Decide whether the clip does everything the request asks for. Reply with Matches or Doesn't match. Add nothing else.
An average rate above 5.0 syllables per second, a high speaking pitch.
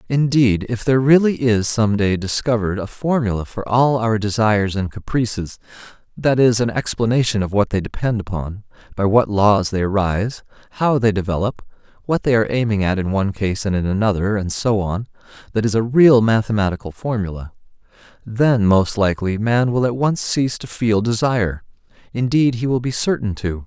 Doesn't match